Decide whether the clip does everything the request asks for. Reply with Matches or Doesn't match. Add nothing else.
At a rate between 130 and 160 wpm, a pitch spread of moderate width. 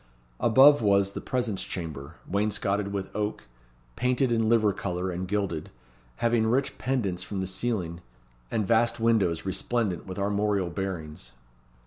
Matches